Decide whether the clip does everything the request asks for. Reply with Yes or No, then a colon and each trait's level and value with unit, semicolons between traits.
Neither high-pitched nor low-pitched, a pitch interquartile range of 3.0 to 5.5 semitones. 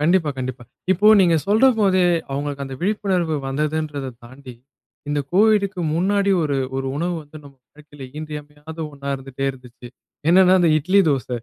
Yes: medium, 150 Hz; average, 5.0 semitones